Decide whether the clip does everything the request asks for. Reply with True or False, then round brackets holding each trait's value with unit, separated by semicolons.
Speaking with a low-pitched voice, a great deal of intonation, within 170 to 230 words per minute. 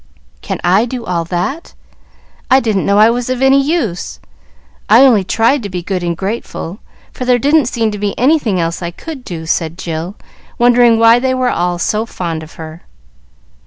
False (215 Hz; 6.0 semitones; 190 wpm)